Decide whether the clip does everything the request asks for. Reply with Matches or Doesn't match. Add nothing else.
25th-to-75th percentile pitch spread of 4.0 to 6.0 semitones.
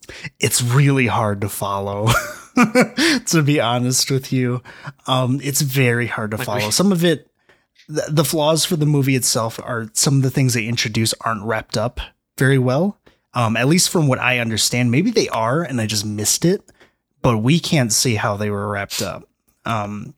Matches